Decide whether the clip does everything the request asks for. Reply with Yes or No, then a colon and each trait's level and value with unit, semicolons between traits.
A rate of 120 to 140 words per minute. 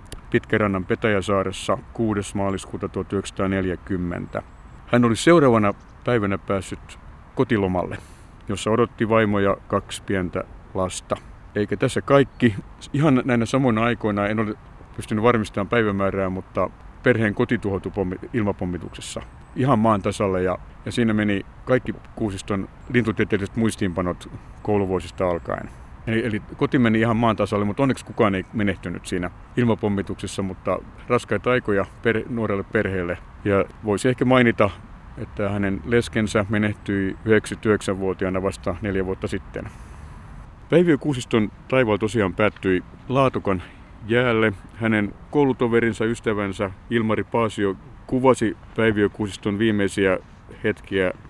No: average, 110 wpm